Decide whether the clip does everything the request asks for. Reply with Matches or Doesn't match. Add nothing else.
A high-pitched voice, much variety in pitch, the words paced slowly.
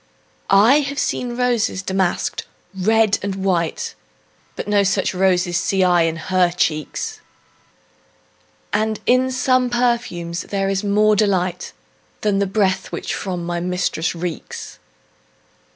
Doesn't match